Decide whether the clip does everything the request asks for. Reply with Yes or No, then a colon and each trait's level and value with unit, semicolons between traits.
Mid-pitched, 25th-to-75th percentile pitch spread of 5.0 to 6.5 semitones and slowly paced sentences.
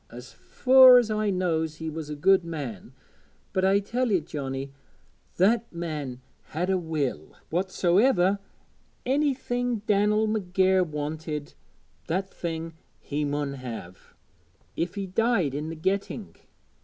Yes: medium, 175 Hz; wide, 5.4 semitones; slow, 130 wpm